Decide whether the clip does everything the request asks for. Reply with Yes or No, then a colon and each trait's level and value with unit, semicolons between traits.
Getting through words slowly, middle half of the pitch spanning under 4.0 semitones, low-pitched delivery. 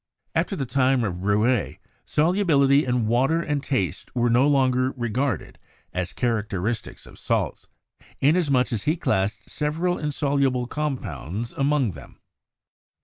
No: slow, 125 wpm; average, 4.4 semitones; low, 130 Hz